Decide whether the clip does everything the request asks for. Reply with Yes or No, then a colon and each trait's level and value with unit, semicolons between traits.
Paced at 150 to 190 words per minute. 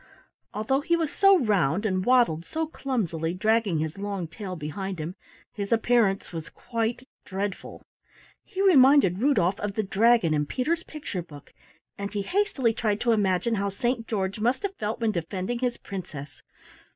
Yes: average, 165 wpm